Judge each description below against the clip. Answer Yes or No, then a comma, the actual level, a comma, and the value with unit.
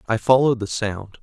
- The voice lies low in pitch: Yes, low, 115 Hz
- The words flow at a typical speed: Yes, average, 195 wpm